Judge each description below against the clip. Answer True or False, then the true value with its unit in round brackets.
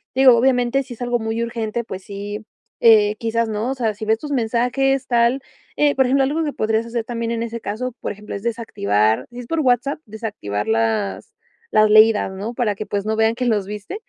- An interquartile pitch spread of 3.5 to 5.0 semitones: False (2.9 semitones)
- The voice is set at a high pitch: True (230 Hz)